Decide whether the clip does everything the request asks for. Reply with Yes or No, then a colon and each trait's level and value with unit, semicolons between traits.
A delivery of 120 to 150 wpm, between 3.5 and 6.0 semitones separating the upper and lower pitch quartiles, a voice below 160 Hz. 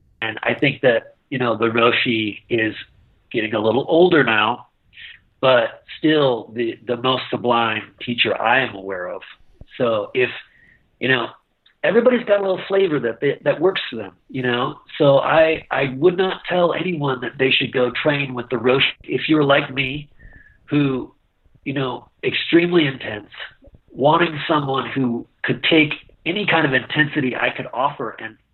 No: average, 165 wpm; average, 4.8 semitones; low, 135 Hz